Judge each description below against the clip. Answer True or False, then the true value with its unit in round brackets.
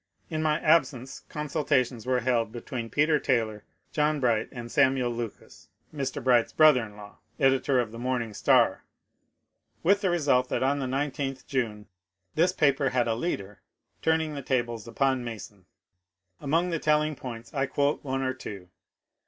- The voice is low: True (130 Hz)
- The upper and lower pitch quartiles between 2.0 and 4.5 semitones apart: True (3.9 semitones)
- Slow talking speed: False (175 wpm)